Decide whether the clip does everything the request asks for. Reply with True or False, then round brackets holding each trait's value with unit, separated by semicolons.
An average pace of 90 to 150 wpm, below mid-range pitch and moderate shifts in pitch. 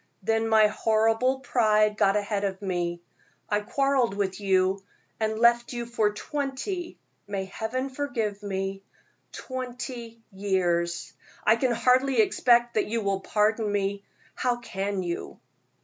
False (135 wpm; 215 Hz; 3.4 semitones)